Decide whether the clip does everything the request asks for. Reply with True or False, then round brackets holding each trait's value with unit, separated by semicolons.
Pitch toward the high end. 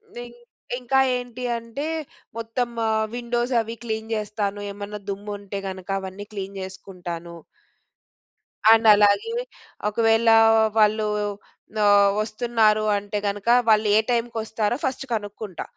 True (215 Hz)